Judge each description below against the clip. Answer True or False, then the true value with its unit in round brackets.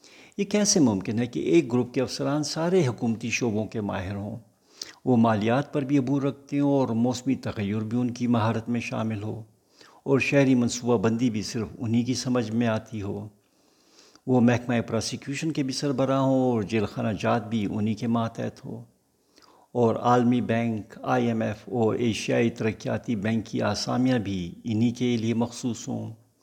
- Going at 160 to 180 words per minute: True (175 wpm)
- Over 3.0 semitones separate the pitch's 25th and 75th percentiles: False (2.4 semitones)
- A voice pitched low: True (120 Hz)